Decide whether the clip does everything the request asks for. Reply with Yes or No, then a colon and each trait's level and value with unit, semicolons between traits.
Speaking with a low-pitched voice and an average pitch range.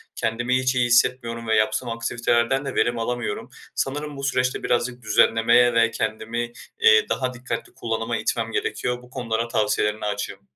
No: low, 120 Hz; narrow, 2.0 semitones